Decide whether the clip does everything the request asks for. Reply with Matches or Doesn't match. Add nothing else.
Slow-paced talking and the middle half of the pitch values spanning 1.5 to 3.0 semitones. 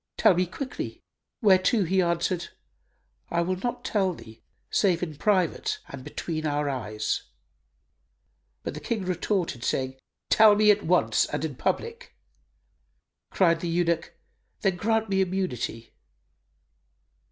Doesn't match